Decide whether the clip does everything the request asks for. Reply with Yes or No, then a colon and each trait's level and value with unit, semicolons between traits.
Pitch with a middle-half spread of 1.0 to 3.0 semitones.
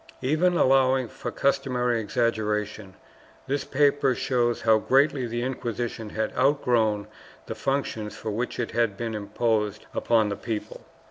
No: average, 3.4 semitones